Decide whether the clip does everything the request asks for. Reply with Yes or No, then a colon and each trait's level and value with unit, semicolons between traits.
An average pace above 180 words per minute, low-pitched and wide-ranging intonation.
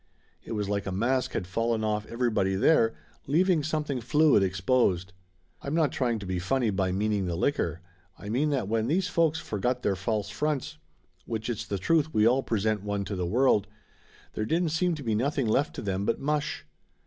Yes: average, 195 wpm; low, 115 Hz; wide, 6.2 semitones